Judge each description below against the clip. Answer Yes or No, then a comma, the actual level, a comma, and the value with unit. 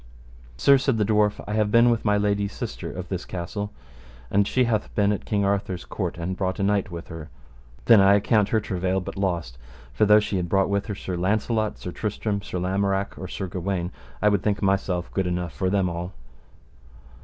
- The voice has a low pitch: Yes, low, 100 Hz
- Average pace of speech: No, fast, 210 wpm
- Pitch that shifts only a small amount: Yes, narrow, 2.2 semitones